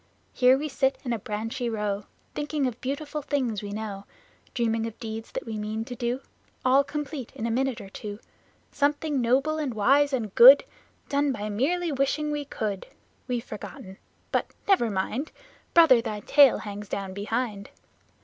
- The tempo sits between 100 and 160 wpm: No, average, 170 wpm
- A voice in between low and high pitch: No, high, 245 Hz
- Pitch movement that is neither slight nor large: Yes, average, 4.7 semitones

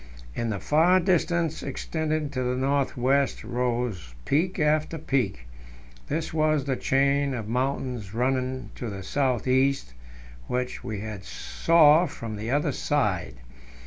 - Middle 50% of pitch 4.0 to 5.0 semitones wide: Yes, average, 4.3 semitones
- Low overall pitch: Yes, low, 130 Hz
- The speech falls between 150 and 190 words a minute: No, average, 140 wpm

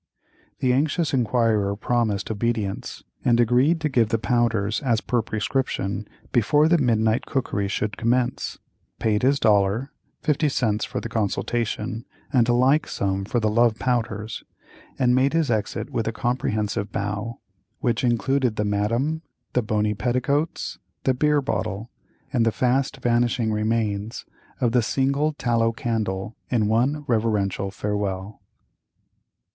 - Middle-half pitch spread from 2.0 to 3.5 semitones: Yes, average, 3.1 semitones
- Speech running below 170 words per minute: Yes, average, 140 wpm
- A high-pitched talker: No, low, 115 Hz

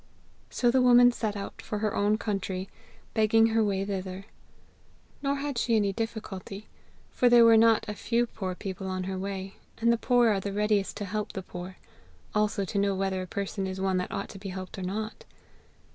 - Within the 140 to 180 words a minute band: No, fast, 205 wpm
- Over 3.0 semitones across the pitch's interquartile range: No, average, 2.7 semitones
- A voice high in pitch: Yes, high, 205 Hz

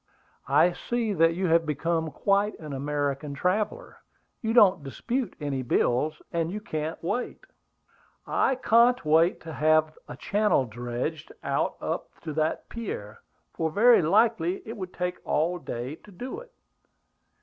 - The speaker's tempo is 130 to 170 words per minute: Yes, average, 150 wpm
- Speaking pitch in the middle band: Yes, medium, 165 Hz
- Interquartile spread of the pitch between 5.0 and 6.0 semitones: Yes, wide, 5.6 semitones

